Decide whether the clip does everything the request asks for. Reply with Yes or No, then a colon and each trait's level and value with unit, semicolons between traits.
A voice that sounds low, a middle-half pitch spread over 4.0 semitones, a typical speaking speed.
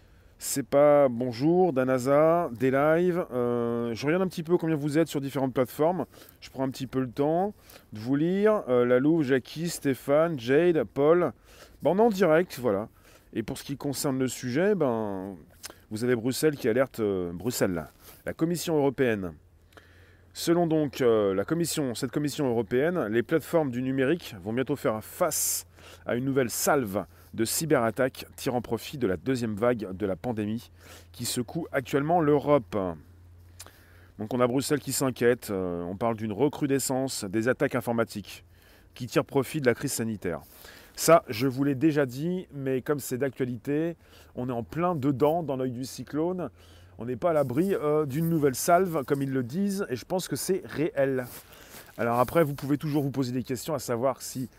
Yes: low, 130 Hz; average, 5.1 semitones; average, 180 wpm